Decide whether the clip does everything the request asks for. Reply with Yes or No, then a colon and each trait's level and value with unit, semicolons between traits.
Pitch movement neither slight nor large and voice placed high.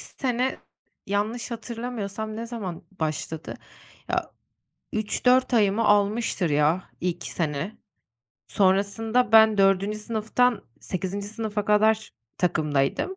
Yes: average, 3.2 semitones; high, 210 Hz